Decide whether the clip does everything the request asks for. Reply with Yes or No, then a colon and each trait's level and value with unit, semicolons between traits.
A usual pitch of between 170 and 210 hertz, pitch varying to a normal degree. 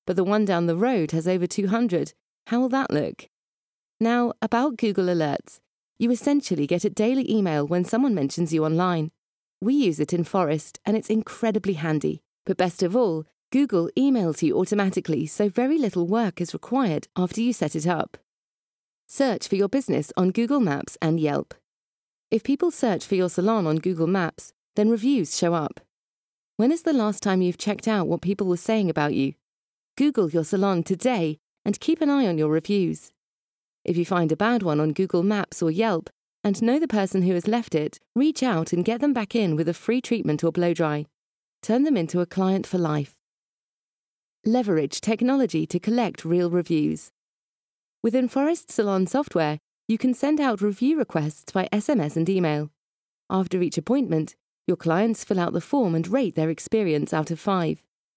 No: high, 190 Hz; wide, 5.9 semitones